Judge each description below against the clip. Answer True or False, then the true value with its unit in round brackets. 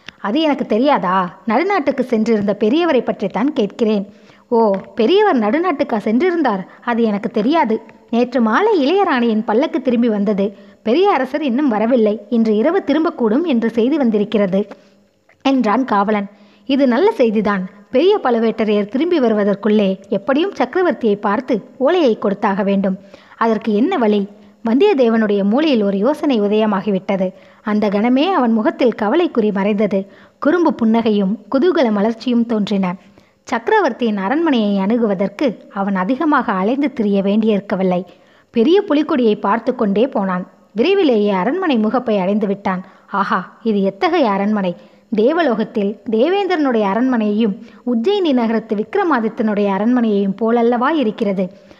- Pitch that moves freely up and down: False (4.5 semitones)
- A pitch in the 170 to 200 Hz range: False (225 Hz)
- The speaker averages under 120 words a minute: True (110 wpm)